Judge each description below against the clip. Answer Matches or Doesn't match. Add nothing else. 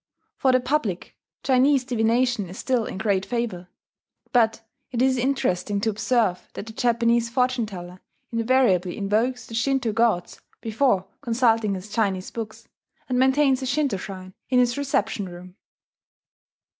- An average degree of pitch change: Matches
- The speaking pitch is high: Matches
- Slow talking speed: Doesn't match